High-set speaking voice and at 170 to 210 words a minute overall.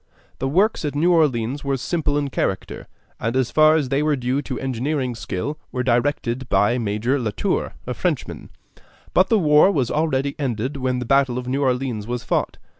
No: low, 135 Hz; average, 190 wpm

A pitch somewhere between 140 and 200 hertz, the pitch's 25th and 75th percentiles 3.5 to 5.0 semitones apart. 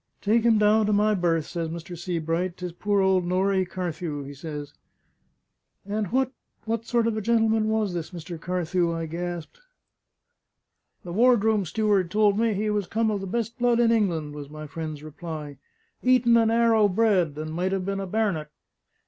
Yes: high, 190 Hz; average, 4.7 semitones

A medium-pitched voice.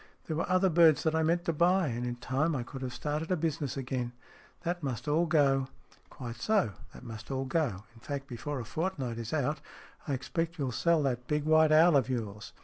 Yes: medium, 145 Hz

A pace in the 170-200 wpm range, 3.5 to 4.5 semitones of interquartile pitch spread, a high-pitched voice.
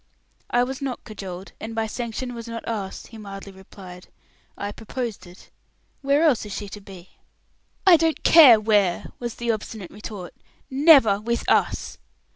No: average, 160 wpm; average, 3.8 semitones; high, 220 Hz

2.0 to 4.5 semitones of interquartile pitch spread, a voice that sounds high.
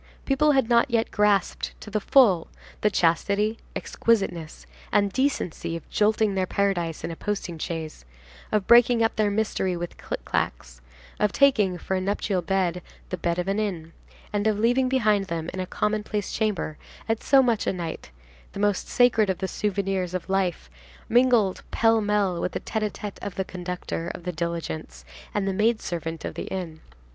Yes: average, 3.6 semitones; high, 195 Hz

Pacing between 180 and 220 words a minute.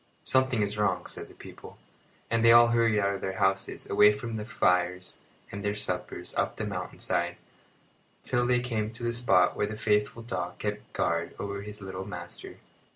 Yes: average, 190 wpm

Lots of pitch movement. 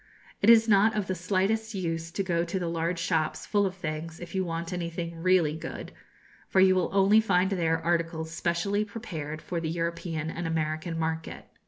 No: narrow, 2.6 semitones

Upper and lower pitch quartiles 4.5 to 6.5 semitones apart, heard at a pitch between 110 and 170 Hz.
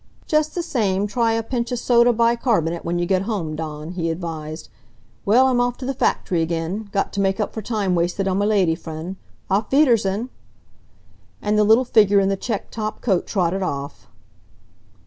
No: average, 5.1 semitones; high, 200 Hz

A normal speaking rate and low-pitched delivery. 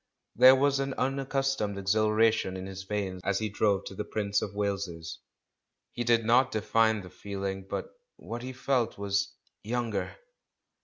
Yes: average, 155 wpm; low, 105 Hz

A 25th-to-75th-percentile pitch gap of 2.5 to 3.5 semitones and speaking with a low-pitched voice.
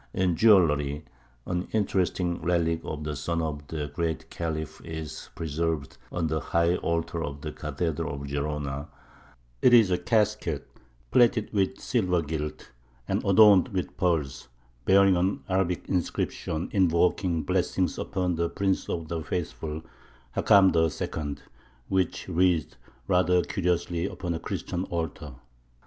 Yes: average, 2.8 semitones; very low, 85 Hz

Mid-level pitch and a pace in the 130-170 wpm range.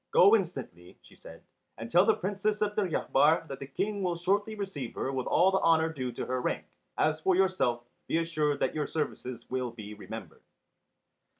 No: medium, 160 Hz; average, 190 wpm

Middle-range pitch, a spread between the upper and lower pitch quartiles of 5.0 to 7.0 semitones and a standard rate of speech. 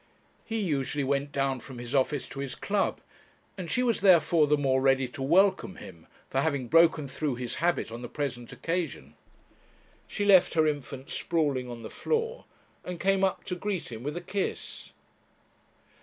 Yes: medium, 145 Hz; average, 5.3 semitones; average, 175 wpm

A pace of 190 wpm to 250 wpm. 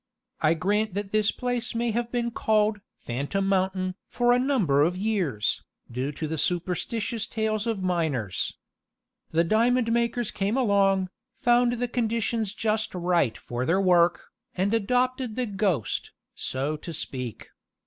No: average, 145 wpm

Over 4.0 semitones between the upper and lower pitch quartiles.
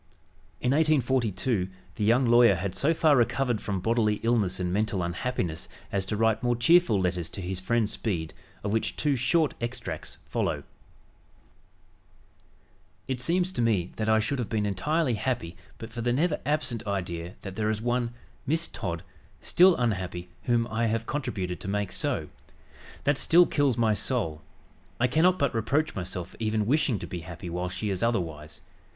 Yes: average, 5.1 semitones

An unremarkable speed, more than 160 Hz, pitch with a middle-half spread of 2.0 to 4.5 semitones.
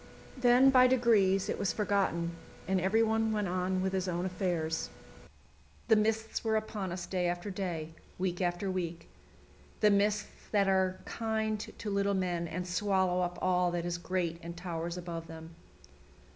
Yes: average, 160 wpm; medium, 185 Hz; average, 3.1 semitones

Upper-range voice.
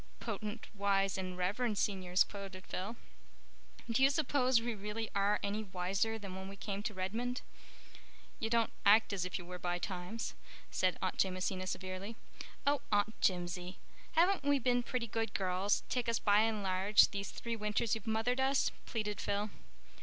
Yes: high, 205 Hz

